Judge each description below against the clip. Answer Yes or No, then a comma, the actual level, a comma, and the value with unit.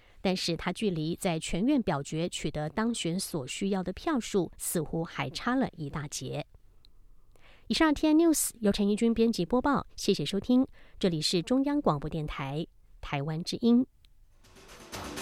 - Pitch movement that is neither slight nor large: No, wide, 6.7 semitones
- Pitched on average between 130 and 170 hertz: No, medium, 180 Hz